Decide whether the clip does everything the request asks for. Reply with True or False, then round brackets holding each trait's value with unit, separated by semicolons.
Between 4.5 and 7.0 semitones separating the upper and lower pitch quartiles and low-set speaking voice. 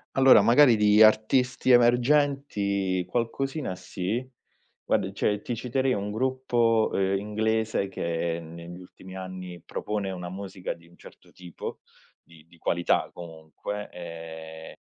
True (5.2 semitones; 100 Hz)